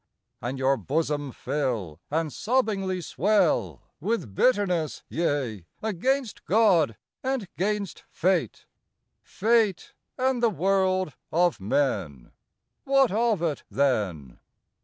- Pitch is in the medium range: Yes, medium, 175 Hz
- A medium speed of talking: No, slow, 100 wpm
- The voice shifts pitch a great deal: Yes, wide, 7.7 semitones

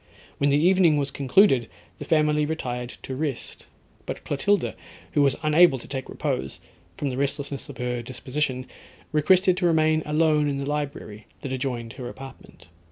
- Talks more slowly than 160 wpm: No, average, 165 wpm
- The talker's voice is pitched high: No, medium, 140 Hz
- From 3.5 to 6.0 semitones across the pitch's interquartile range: No, average, 3.1 semitones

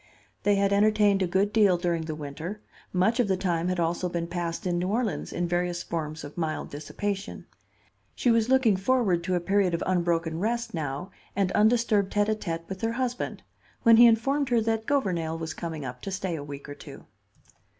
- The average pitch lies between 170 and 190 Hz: Yes, medium, 185 Hz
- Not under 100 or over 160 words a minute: No, average, 200 wpm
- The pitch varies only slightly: No, average, 4.3 semitones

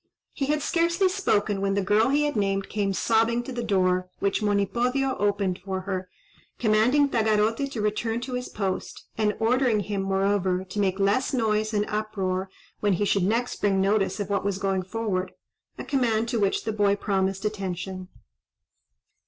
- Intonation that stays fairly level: No, average, 3.0 semitones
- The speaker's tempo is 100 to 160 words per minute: No, average, 170 wpm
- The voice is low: No, high, 210 Hz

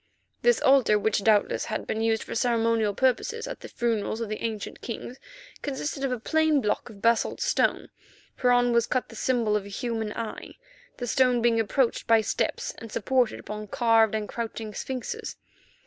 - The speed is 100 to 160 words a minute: No, average, 180 wpm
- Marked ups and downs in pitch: No, narrow, 2.5 semitones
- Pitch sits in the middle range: No, high, 230 Hz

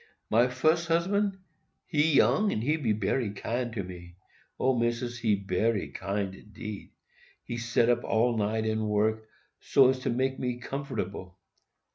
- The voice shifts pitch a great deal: No, average, 3.8 semitones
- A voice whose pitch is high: No, low, 120 Hz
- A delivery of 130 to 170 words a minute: Yes, average, 140 wpm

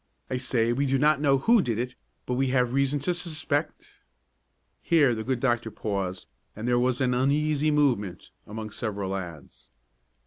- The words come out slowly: No, average, 175 wpm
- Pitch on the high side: No, low, 125 Hz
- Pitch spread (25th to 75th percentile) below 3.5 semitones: No, average, 4.1 semitones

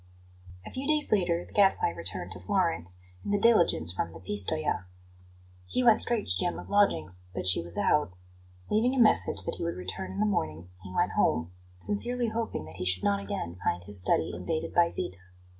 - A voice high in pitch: No, low, 100 Hz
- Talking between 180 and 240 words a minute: Yes, average, 190 wpm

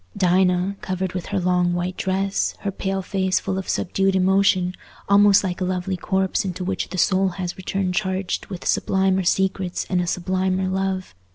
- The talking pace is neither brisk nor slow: Yes, average, 175 wpm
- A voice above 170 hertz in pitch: Yes, high, 190 Hz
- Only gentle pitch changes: Yes, narrow, 1.0 semitones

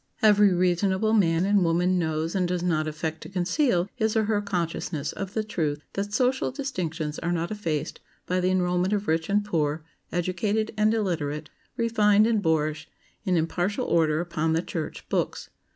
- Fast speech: No, average, 170 wpm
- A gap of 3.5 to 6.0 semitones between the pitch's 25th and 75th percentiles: Yes, average, 4.2 semitones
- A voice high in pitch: No, medium, 180 Hz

